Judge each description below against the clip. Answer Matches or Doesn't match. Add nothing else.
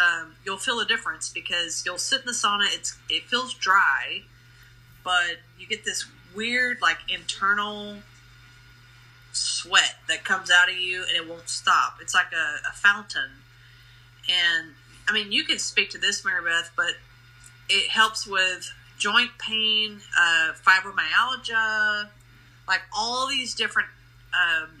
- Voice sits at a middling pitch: Matches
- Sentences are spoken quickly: Doesn't match